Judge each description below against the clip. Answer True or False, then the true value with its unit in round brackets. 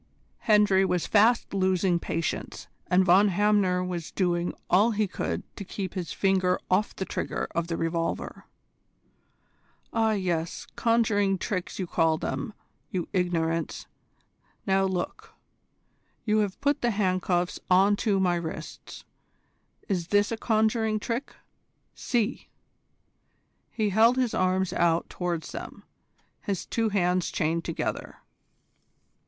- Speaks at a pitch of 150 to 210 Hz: True (190 Hz)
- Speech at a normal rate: False (125 wpm)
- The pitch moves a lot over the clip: False (3.1 semitones)